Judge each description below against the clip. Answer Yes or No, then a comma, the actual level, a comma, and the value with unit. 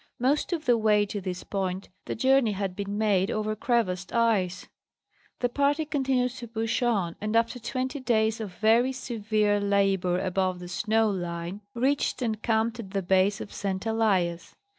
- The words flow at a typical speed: Yes, average, 170 wpm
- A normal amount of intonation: Yes, average, 3.7 semitones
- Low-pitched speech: No, high, 215 Hz